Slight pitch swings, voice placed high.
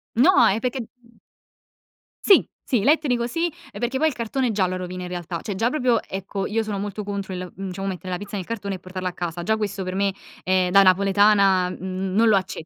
No: average, 3.6 semitones; high, 195 Hz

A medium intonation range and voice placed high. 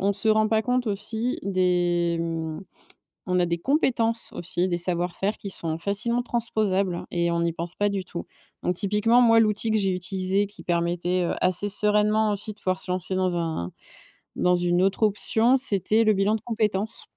Yes: average, 3.6 semitones; high, 195 Hz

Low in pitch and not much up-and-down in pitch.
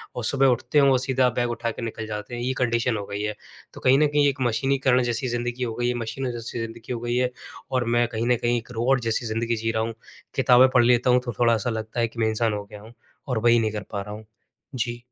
Yes: low, 120 Hz; narrow, 1.8 semitones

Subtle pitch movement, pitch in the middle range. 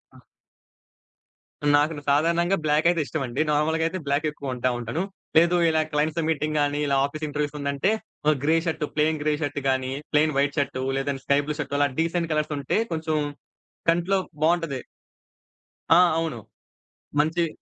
Yes: narrow, 2.3 semitones; medium, 150 Hz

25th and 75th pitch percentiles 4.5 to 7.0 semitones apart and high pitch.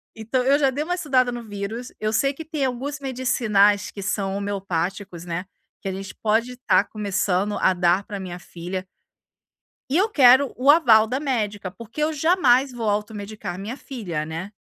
Yes: average, 5.1 semitones; high, 220 Hz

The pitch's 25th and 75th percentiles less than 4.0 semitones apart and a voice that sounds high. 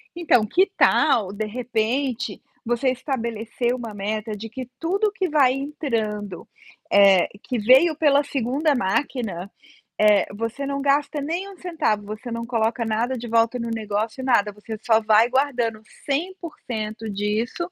No: average, 4.4 semitones; high, 235 Hz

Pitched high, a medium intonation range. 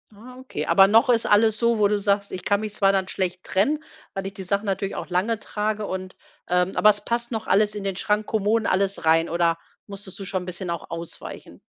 No: high, 200 Hz; narrow, 2.3 semitones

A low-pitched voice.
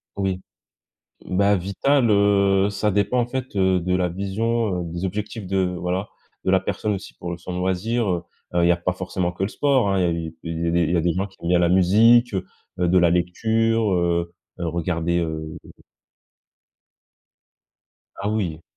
Yes: very low, 95 Hz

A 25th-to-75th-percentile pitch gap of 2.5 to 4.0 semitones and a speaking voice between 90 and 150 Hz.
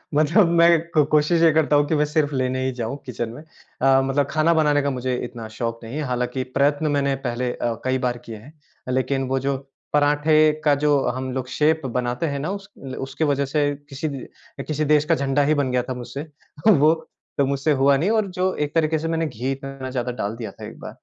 Yes: average, 3.0 semitones; medium, 140 Hz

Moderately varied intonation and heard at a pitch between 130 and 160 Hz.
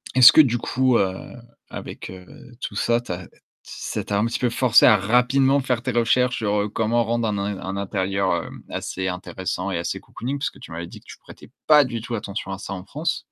No: average, 4.3 semitones; low, 110 Hz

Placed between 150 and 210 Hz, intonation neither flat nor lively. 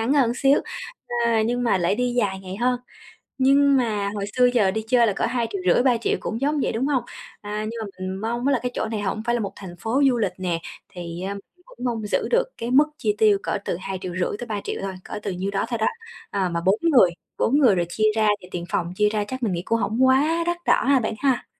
No: high, 220 Hz; average, 4.2 semitones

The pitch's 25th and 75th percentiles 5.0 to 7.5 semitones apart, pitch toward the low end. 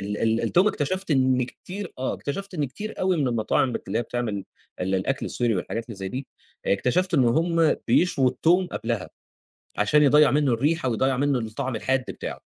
Yes: wide, 5.6 semitones; low, 130 Hz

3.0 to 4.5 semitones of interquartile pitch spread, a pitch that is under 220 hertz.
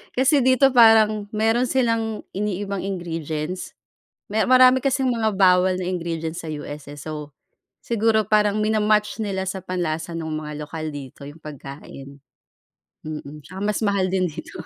No: wide, 5.6 semitones; high, 190 Hz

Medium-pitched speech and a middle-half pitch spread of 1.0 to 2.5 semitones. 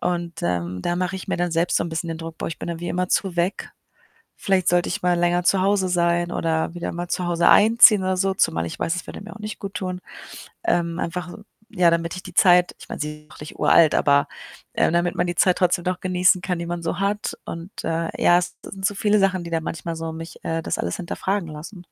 Yes: medium, 175 Hz; narrow, 1.8 semitones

